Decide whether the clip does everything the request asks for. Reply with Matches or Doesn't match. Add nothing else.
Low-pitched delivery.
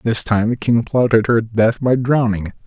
Matches